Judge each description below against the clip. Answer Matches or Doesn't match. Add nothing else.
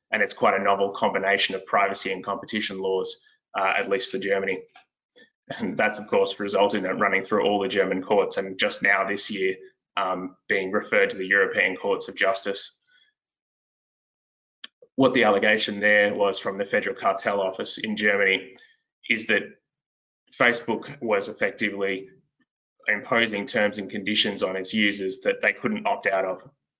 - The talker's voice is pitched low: Matches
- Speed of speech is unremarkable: Matches